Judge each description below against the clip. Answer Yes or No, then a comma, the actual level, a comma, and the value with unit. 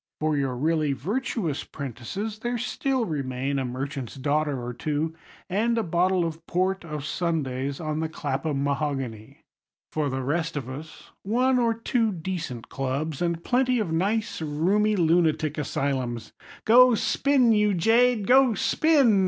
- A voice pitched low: No, medium, 160 Hz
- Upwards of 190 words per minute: No, average, 145 wpm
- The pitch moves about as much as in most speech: No, wide, 7.3 semitones